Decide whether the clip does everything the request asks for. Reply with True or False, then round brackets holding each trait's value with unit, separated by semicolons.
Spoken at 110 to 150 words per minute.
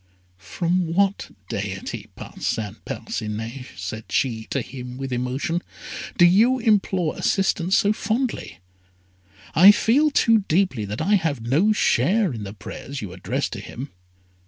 True (135 wpm)